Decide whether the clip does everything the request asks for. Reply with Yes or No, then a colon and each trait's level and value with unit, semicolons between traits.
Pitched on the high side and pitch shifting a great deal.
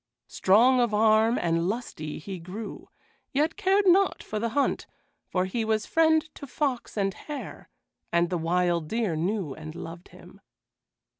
Yes: high, 215 Hz; wide, 6.7 semitones